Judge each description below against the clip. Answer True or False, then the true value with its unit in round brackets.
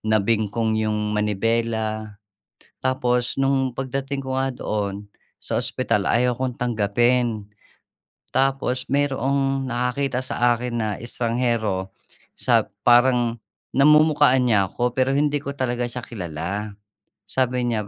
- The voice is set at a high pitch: False (120 Hz)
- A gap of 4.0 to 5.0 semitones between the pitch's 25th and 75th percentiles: False (3.3 semitones)